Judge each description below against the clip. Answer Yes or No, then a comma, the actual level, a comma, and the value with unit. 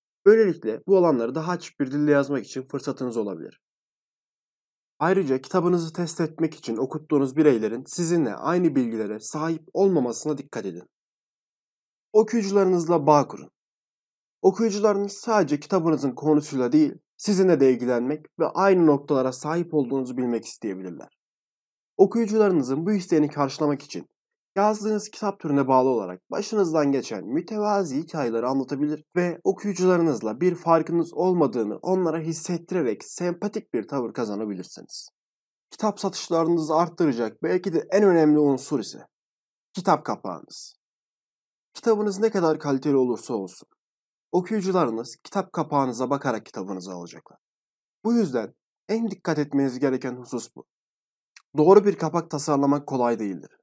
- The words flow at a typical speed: Yes, average, 120 wpm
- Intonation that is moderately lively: No, wide, 5.7 semitones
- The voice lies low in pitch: No, medium, 160 Hz